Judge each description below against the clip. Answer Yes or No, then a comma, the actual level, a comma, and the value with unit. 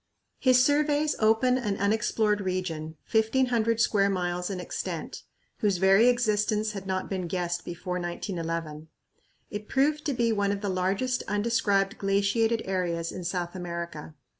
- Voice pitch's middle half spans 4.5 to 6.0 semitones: No, average, 4.0 semitones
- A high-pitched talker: Yes, high, 200 Hz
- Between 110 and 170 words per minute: Yes, average, 140 wpm